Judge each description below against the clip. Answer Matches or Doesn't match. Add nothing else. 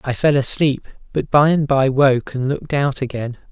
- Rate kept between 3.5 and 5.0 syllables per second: Matches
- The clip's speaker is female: Doesn't match